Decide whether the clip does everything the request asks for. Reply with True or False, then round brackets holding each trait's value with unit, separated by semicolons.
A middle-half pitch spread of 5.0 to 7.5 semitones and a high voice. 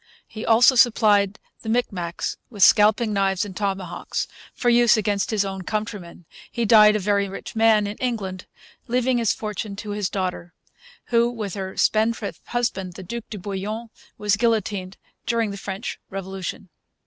False (2.8 semitones; 210 Hz)